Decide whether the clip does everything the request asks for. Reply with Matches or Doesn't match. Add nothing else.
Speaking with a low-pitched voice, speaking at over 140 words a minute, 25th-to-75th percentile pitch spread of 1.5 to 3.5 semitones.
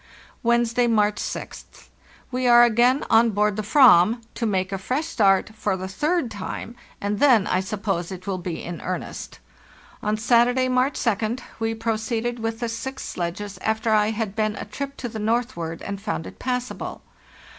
Doesn't match